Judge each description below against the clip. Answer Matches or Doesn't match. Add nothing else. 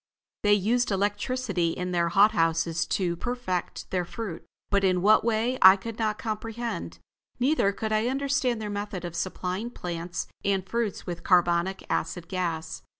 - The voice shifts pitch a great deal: Doesn't match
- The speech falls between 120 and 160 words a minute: Matches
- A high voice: Matches